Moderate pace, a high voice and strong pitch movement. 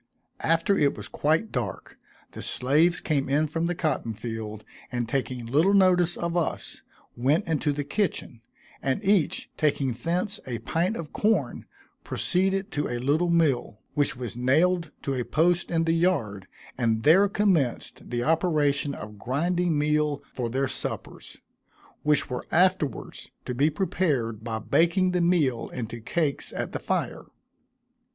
No: average, 150 wpm; medium, 150 Hz; wide, 5.7 semitones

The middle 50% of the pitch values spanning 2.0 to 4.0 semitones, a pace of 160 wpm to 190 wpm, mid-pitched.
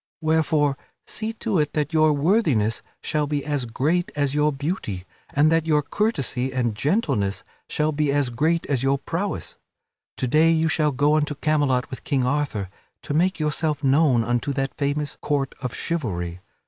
Yes: average, 3.0 semitones; average, 170 wpm; medium, 145 Hz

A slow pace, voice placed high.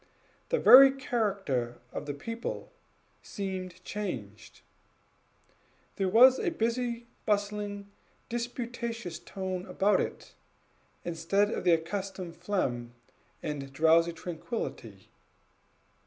Yes: slow, 95 wpm; high, 195 Hz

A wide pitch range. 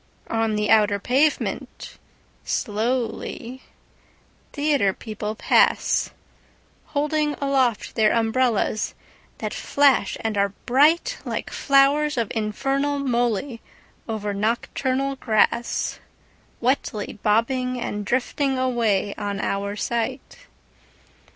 No: average, 4.4 semitones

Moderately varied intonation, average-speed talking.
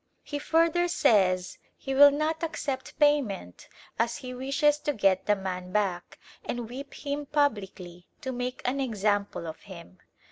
No: wide, 7.0 semitones; average, 150 wpm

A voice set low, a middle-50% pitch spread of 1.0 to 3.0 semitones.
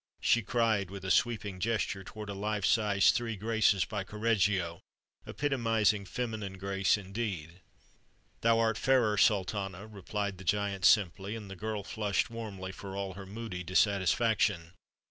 Yes: low, 100 Hz; narrow, 2.5 semitones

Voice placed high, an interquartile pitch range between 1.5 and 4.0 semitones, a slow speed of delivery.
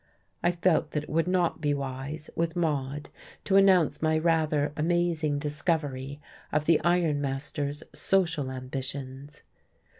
No: medium, 150 Hz; average, 2.9 semitones; slow, 130 wpm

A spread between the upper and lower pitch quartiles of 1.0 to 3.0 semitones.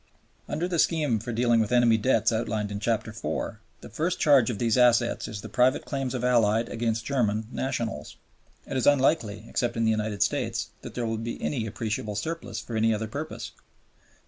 Yes: narrow, 2.6 semitones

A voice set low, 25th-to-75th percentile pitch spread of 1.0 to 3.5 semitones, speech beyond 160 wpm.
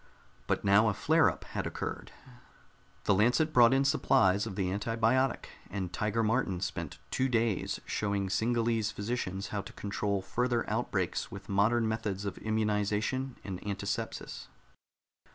No: low, 105 Hz; average, 2.8 semitones; slow, 135 wpm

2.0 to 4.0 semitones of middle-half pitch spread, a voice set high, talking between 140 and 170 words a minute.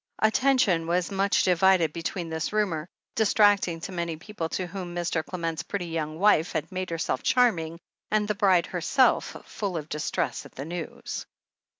No: average, 3.4 semitones; medium, 175 Hz; average, 165 wpm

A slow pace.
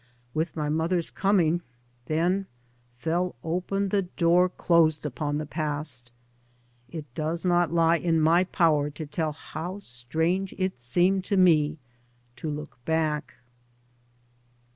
Yes: slow, 125 wpm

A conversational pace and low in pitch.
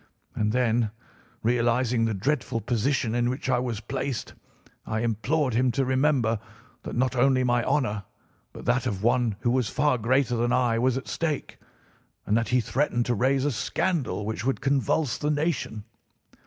Yes: average, 170 wpm; low, 125 Hz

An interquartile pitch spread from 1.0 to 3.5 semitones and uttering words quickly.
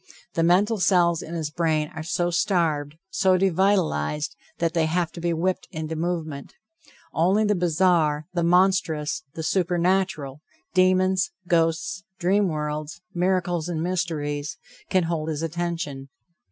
No: average, 2.7 semitones; slow, 135 wpm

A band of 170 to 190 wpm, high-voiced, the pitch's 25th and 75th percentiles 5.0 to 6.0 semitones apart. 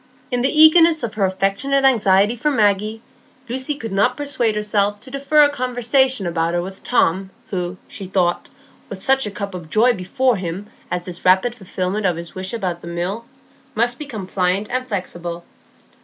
Yes: average, 180 wpm; high, 205 Hz; average, 5.3 semitones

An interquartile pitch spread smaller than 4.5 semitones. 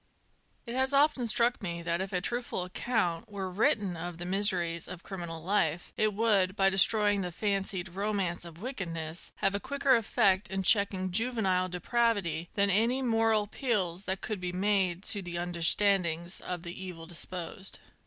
Yes: average, 3.4 semitones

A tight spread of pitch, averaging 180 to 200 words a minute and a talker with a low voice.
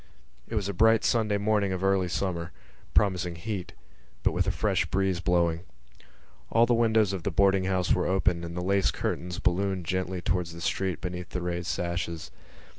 Yes: narrow, 2.2 semitones; average, 185 wpm; very low, 95 Hz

